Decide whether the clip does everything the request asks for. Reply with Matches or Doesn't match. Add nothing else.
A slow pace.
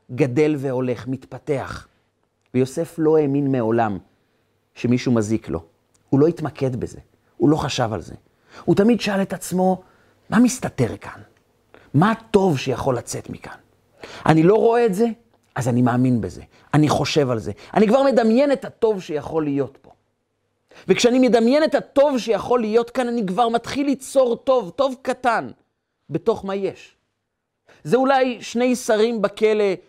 Doesn't match